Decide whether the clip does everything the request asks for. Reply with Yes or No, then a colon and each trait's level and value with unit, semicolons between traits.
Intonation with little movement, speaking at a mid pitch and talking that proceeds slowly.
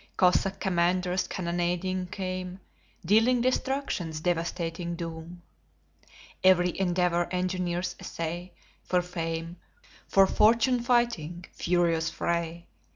Yes: narrow, 1.6 semitones; medium, 180 Hz; slow, 90 wpm